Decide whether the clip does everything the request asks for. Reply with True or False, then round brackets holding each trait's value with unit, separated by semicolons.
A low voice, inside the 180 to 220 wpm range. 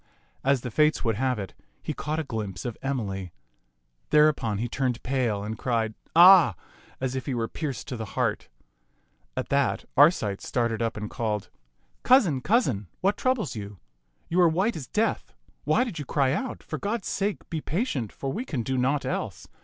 True (130 Hz; 195 wpm)